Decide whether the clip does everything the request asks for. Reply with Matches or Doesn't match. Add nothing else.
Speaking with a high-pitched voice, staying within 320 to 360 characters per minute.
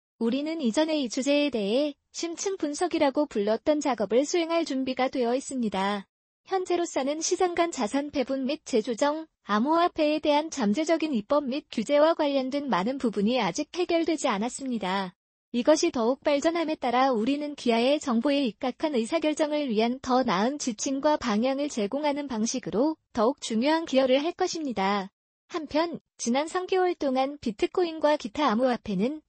Matches